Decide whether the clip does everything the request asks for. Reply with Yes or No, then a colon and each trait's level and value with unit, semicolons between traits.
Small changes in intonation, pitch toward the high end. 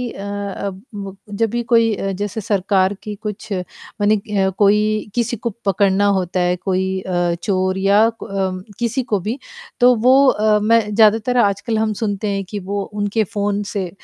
Yes: narrow, 2.2 semitones; high, 205 Hz